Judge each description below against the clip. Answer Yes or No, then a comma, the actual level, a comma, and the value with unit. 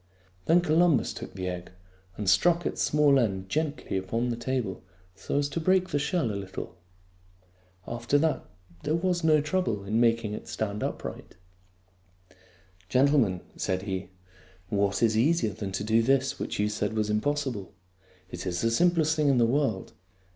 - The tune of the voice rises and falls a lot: Yes, wide, 7.2 semitones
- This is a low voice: Yes, low, 115 Hz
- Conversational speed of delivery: Yes, average, 170 wpm